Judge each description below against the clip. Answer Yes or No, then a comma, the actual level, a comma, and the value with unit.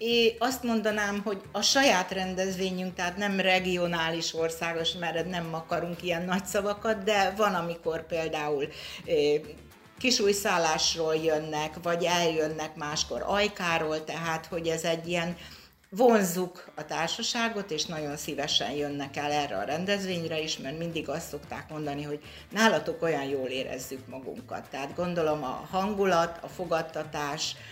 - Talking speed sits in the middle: Yes, average, 140 wpm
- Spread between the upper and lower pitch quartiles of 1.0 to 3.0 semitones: No, average, 3.7 semitones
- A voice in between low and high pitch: Yes, medium, 170 Hz